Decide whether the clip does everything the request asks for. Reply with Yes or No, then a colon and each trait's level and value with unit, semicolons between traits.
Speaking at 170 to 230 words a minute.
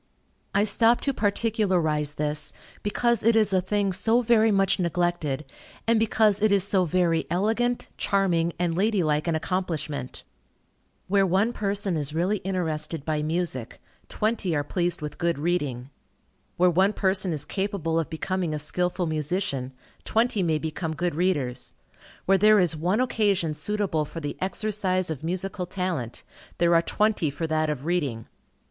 No: average, 155 wpm